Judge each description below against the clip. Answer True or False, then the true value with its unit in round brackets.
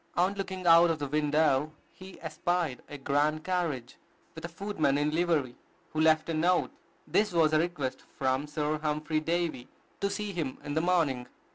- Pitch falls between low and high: True (155 Hz)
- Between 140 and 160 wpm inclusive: False (175 wpm)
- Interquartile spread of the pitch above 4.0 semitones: False (3.0 semitones)